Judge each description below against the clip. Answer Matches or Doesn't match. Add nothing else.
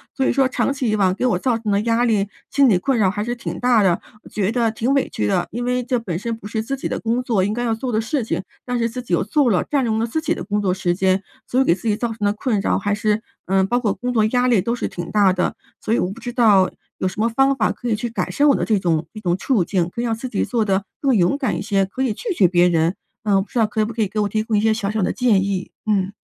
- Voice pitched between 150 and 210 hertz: Doesn't match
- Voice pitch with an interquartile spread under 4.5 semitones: Matches